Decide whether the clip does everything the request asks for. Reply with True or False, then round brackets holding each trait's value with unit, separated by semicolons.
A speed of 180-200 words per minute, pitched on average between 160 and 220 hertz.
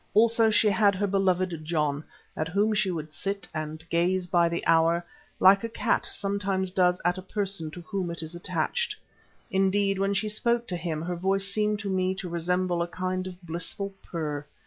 True (190 wpm; 185 Hz)